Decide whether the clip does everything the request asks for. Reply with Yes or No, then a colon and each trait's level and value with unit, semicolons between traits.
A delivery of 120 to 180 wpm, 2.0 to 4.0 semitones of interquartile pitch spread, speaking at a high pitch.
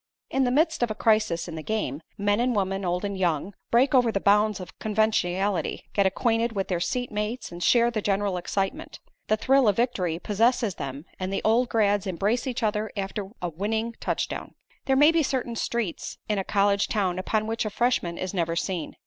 No: fast, 205 wpm; average, 3.7 semitones; high, 210 Hz